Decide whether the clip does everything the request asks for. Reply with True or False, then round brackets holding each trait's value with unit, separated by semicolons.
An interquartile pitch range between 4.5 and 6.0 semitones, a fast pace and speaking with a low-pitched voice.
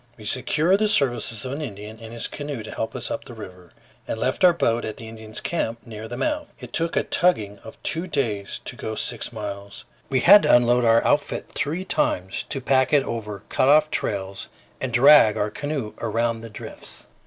True (4.8 semitones; 210 wpm; 115 Hz)